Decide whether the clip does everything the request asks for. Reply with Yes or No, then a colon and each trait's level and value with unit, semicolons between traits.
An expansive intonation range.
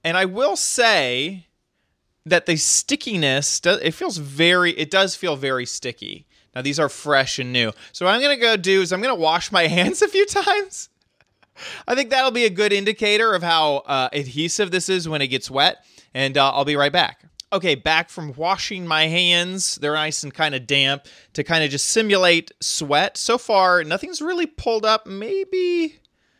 Yes: wide, 6.9 semitones